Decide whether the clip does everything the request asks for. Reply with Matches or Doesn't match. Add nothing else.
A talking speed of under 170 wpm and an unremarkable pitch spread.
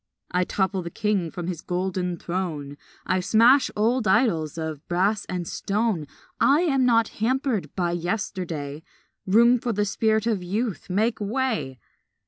Matches